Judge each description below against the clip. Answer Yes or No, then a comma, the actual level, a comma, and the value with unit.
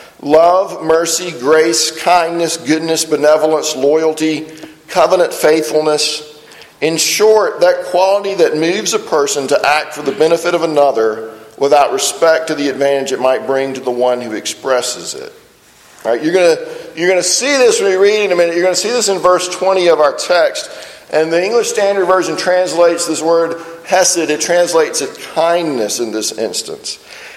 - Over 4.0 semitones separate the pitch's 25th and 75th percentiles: No, average, 3.5 semitones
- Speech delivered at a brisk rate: No, average, 175 wpm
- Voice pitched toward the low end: No, medium, 165 Hz